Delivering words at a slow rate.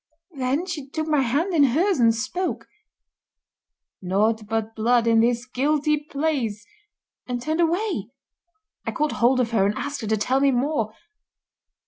No: average, 155 wpm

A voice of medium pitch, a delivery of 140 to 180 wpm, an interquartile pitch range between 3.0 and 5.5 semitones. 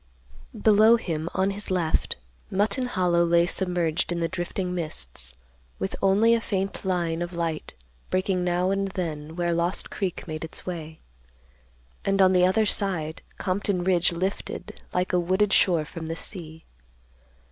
No: medium, 180 Hz; average, 155 wpm; narrow, 2.5 semitones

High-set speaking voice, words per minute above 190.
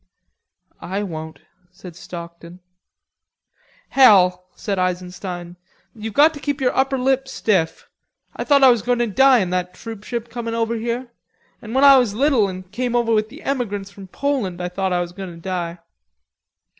No: high, 210 Hz; average, 170 wpm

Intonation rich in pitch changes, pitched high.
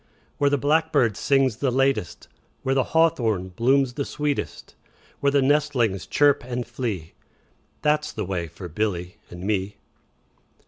No: wide, 6.0 semitones; low, 125 Hz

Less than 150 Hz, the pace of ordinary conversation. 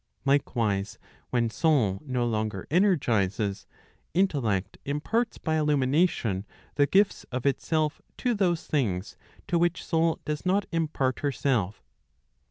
No: medium, 140 Hz; slow, 115 wpm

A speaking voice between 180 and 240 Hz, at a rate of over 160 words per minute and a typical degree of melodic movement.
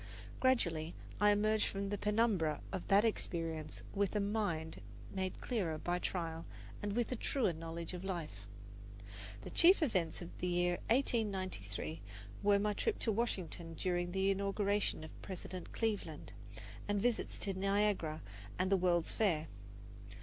No: high, 190 Hz; average, 145 wpm; average, 3.7 semitones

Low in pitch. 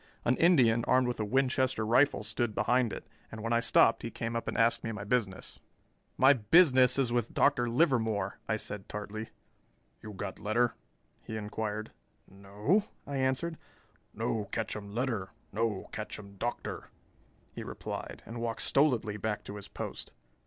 Yes: low, 115 Hz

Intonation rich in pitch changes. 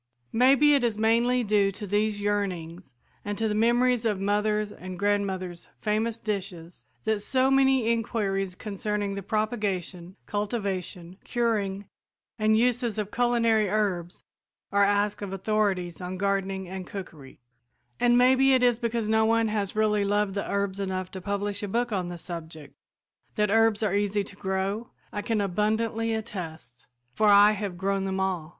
No: narrow, 2.6 semitones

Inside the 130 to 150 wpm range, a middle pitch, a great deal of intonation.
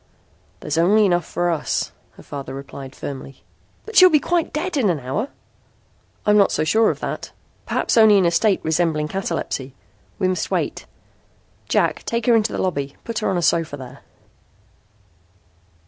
No: average, 170 wpm; medium, 175 Hz; wide, 6.3 semitones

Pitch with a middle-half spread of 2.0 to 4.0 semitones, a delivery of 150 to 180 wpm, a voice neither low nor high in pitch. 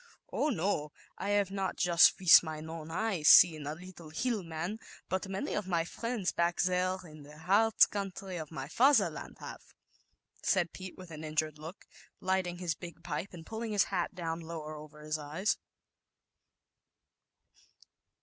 Yes: average, 3.5 semitones; average, 165 wpm; medium, 175 Hz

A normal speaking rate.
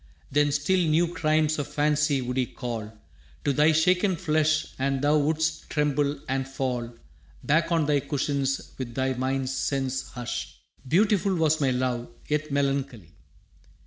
Yes: average, 145 wpm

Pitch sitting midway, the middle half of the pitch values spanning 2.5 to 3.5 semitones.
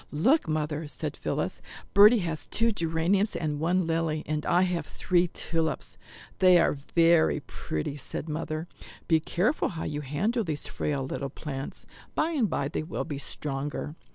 Yes: medium, 160 Hz; average, 3.2 semitones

